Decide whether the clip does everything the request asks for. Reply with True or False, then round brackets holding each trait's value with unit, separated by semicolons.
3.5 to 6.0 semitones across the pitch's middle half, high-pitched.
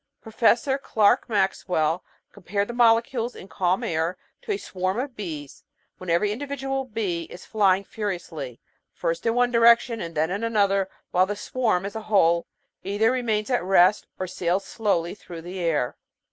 True (4.5 semitones; 200 Hz)